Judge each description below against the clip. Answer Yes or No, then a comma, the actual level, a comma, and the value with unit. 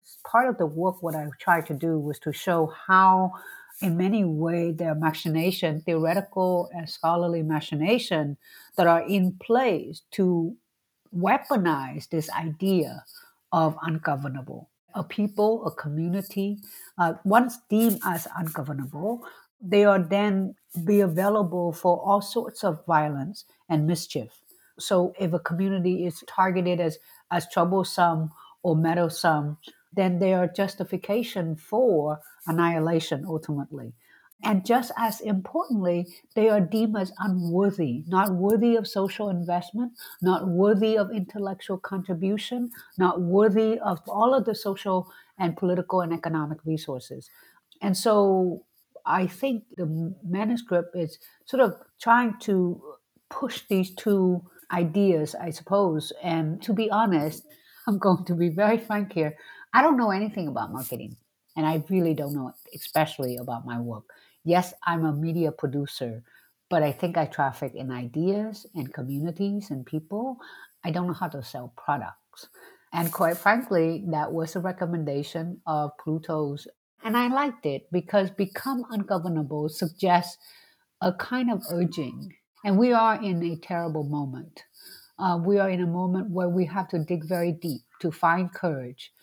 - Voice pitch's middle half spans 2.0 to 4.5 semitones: Yes, average, 3.8 semitones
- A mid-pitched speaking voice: Yes, medium, 180 Hz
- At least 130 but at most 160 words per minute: Yes, average, 145 wpm